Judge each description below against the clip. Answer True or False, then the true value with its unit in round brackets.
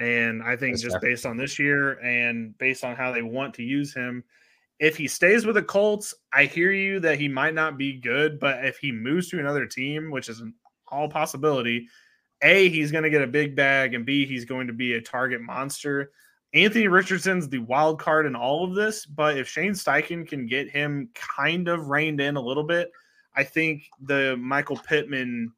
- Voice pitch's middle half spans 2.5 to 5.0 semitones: True (3.5 semitones)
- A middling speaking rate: False (210 wpm)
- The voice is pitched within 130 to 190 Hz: True (140 Hz)